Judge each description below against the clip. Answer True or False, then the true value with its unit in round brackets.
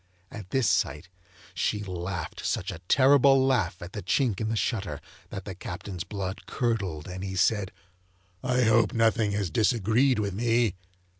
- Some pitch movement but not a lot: True (4.1 semitones)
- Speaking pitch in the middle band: False (105 Hz)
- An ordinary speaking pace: True (160 wpm)